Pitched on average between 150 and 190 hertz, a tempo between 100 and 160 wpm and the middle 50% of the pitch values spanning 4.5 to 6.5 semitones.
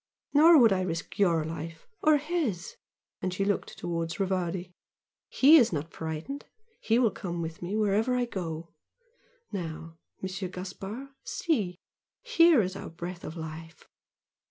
Yes: medium, 185 Hz; average, 145 wpm; wide, 5.6 semitones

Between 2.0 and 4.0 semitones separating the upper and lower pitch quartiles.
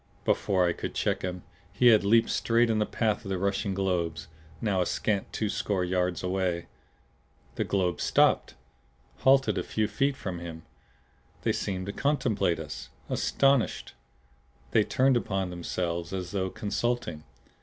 Yes: average, 3.7 semitones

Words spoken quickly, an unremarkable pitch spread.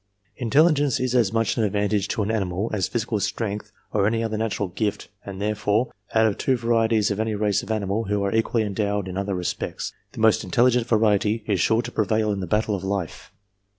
No: fast, 215 wpm; narrow, 2.0 semitones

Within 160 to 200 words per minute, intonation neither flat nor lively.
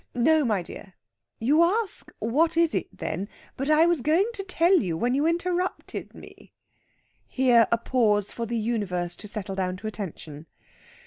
No: average, 170 wpm; wide, 8.3 semitones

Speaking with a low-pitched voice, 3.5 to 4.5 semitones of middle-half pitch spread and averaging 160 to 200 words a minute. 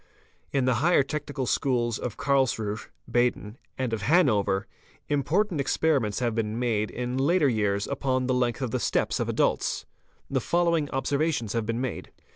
Yes: low, 125 Hz; average, 3.8 semitones; average, 170 wpm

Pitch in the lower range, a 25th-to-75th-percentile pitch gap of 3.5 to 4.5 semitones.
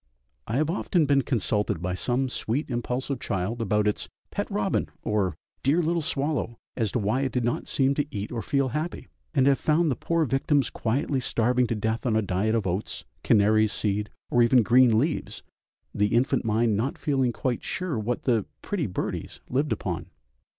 Yes: low, 120 Hz; average, 4.1 semitones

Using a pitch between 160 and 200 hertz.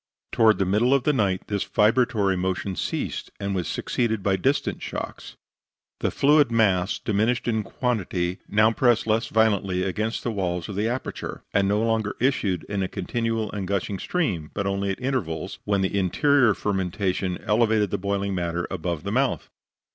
No: low, 100 Hz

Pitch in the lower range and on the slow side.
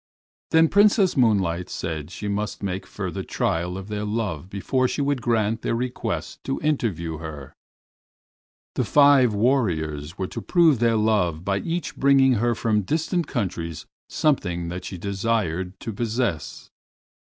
No: low, 105 Hz; average, 145 wpm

